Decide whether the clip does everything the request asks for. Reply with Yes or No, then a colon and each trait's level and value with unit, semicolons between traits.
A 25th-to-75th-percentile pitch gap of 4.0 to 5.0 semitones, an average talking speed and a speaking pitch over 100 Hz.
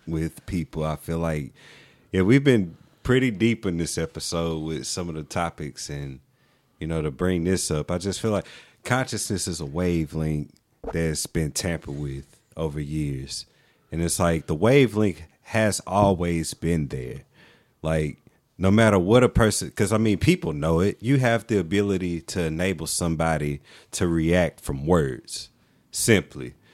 No: average, 4.5 semitones; average, 160 wpm; very low, 85 Hz